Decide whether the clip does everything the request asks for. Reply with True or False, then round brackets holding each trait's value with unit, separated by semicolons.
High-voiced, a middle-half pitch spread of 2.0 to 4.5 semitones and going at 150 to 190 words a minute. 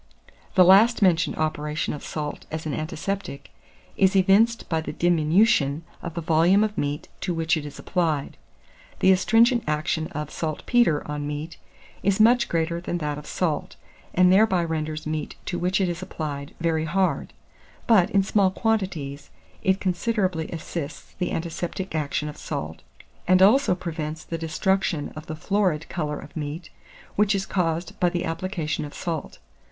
False (170 Hz; 3.7 semitones; 160 wpm)